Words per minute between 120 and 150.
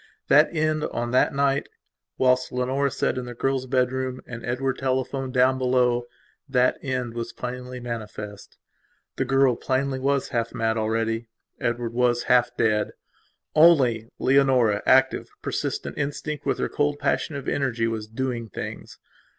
Yes: average, 140 wpm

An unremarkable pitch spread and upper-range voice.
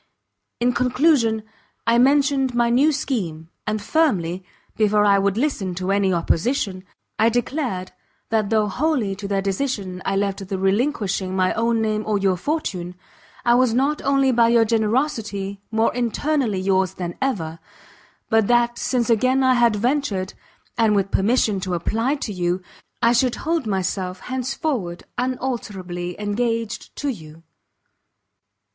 Yes: average, 4.7 semitones; high, 220 Hz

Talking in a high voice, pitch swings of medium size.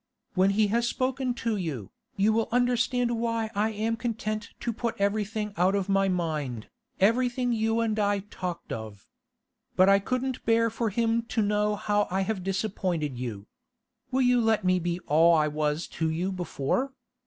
Yes: high, 210 Hz; average, 4.1 semitones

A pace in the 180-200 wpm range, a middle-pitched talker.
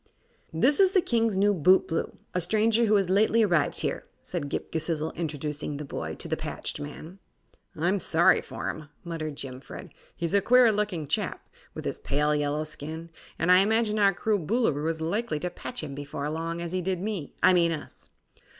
Yes: average, 190 wpm; medium, 170 Hz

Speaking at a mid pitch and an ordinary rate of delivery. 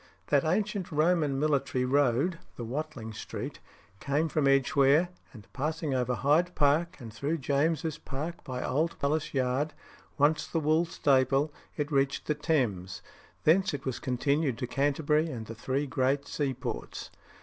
Yes: medium, 145 Hz; average, 150 wpm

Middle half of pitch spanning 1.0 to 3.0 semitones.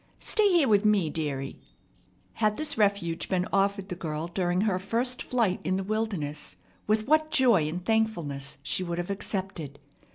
No: average, 4.4 semitones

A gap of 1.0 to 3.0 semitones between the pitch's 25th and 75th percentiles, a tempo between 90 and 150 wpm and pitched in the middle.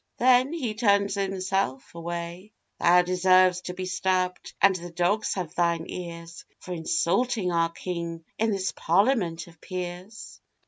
Yes: narrow, 2.5 semitones; average, 140 wpm; medium, 180 Hz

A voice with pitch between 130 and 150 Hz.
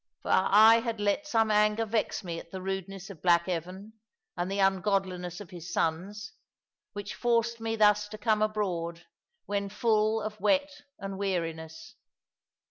No: high, 200 Hz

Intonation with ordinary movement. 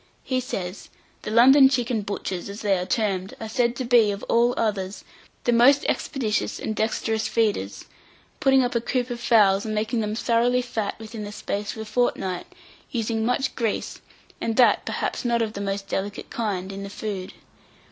Yes: average, 3.0 semitones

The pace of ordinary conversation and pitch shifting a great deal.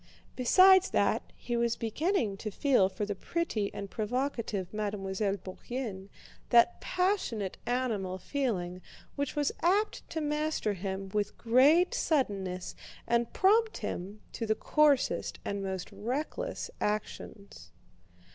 No: slow, 120 wpm; wide, 6.8 semitones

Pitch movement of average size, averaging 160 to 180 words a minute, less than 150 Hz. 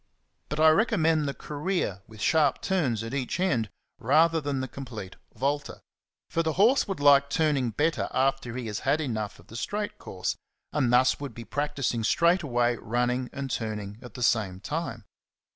Yes: average, 5.0 semitones; average, 175 wpm; low, 135 Hz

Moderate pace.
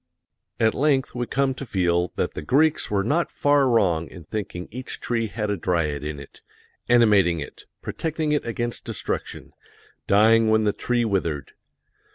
Yes: average, 165 wpm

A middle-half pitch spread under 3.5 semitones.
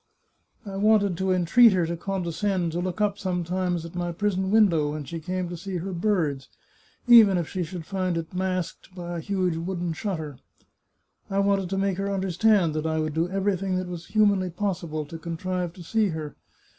Yes: narrow, 2.6 semitones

